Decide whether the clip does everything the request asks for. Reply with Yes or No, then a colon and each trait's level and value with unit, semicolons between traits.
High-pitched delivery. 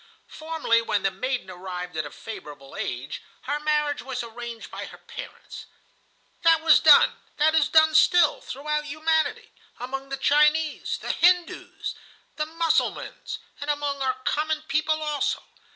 Yes: very high, 295 Hz